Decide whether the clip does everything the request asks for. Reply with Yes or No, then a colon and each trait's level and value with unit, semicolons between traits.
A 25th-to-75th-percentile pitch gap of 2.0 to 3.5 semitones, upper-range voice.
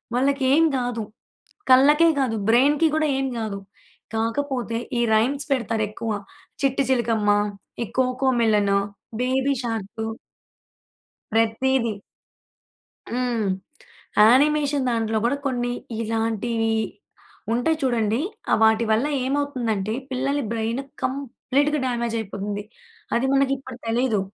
Yes: average, 3.2 semitones; high, 245 Hz